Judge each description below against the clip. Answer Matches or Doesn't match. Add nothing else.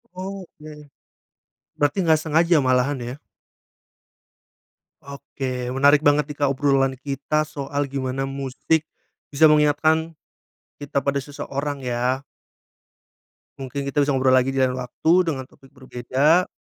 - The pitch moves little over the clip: Matches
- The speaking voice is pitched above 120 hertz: Matches